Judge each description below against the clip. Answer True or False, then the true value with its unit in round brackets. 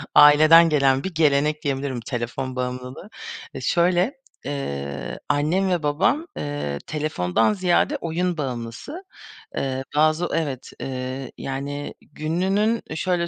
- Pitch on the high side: False (145 Hz)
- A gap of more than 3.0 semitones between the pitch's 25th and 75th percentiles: True (4.6 semitones)